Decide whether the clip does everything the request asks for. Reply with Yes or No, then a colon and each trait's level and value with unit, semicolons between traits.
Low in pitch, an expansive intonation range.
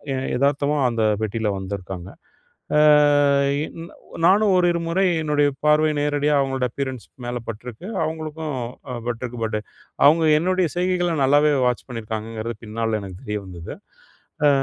Yes: low, 130 Hz; wide, 5.7 semitones